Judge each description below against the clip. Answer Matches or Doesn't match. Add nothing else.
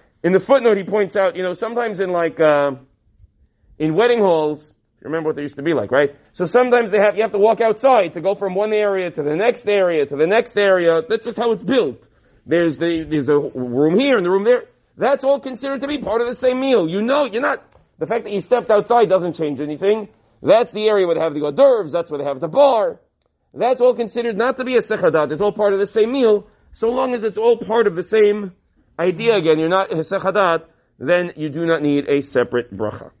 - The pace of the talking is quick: Matches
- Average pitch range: Doesn't match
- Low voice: Doesn't match